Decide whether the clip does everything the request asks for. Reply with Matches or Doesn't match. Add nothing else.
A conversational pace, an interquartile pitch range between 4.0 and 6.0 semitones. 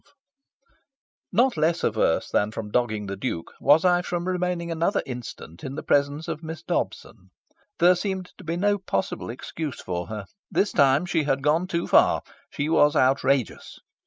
Matches